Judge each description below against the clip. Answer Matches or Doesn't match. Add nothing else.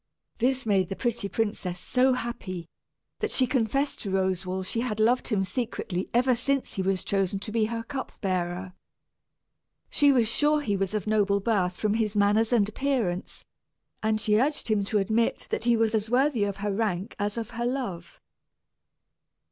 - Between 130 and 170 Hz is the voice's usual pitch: Doesn't match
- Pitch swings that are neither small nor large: Matches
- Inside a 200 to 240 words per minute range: Doesn't match